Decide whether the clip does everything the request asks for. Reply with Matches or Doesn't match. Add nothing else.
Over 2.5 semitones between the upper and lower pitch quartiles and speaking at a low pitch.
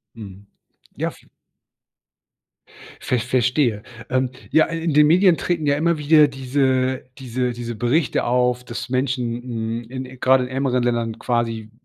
Matches